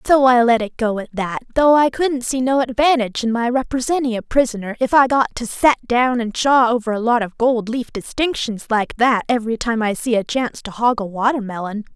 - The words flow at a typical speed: No, fast, 225 wpm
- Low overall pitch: No, high, 240 Hz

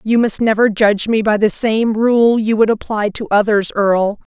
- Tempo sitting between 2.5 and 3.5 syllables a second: No, 4.9 syllables/s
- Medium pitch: No, high, 215 Hz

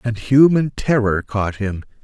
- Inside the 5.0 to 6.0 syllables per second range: No, 3.9 syllables/s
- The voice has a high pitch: No, low, 115 Hz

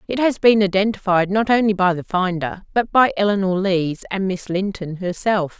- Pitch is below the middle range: No, high, 195 Hz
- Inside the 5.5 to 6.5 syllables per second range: No, 5.0 syllables/s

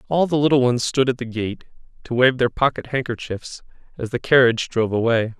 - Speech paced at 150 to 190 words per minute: No, average, 200 wpm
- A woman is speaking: No, male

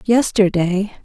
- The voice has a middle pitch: No, high, 200 Hz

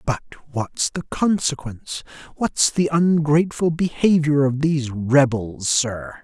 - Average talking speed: No, slow, 115 wpm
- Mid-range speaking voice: Yes, medium, 145 Hz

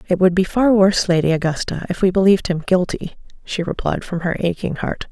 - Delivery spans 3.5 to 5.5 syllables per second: No, 5.8 syllables/s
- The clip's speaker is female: Yes, female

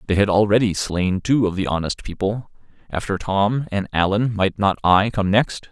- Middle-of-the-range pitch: No, low, 100 Hz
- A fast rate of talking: No, average, 190 wpm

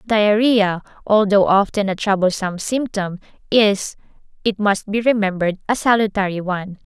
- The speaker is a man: No, female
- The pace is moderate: No, slow, 120 wpm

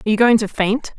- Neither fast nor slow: No, fast, 305 wpm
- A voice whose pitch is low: No, high, 220 Hz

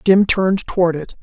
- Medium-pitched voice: Yes, medium, 180 Hz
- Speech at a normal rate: Yes, average, 195 wpm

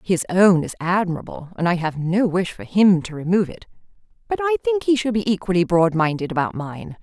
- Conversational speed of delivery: No, fast, 215 wpm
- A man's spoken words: No, female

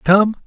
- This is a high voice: Yes, high, 200 Hz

